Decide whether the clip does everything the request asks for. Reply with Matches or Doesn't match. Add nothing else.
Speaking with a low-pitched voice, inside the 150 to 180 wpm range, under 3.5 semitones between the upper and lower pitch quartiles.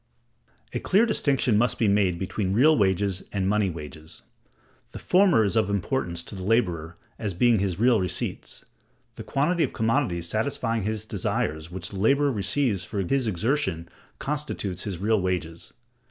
Doesn't match